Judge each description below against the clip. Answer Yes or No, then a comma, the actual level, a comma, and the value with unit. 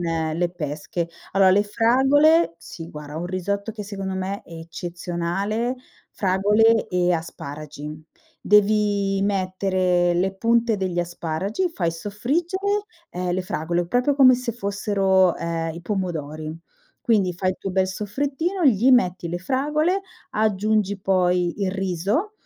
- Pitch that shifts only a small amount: No, average, 3.9 semitones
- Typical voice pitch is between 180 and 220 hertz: Yes, high, 190 Hz